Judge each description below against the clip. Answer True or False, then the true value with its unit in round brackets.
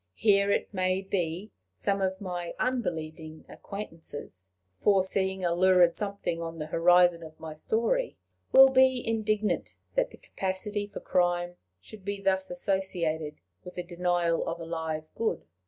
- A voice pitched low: False (185 Hz)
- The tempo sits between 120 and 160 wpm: True (145 wpm)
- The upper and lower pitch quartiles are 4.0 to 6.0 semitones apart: False (3.3 semitones)